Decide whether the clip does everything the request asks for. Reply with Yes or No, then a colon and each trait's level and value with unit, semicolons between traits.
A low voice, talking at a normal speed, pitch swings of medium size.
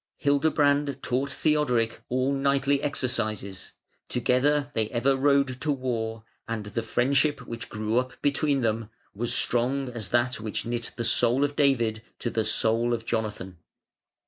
Yes: low, 125 Hz; average, 145 wpm; average, 3.6 semitones